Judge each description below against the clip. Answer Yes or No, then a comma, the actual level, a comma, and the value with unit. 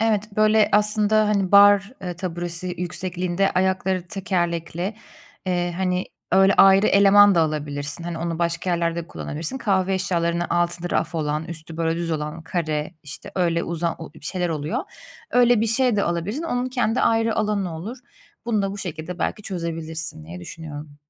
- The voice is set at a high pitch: No, medium, 180 Hz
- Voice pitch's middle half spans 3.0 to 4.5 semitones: Yes, average, 3.5 semitones